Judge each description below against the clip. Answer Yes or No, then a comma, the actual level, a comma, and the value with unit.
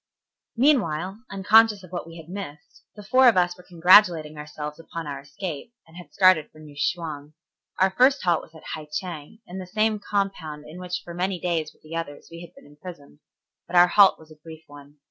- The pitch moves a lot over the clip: No, average, 3.7 semitones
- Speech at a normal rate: No, fast, 210 wpm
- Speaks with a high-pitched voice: No, medium, 175 Hz